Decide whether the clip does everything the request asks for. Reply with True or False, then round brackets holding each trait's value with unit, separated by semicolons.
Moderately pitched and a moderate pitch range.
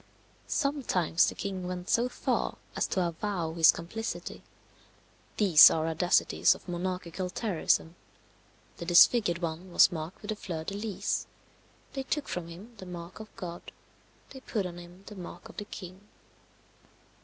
True (180 Hz; 3.3 semitones)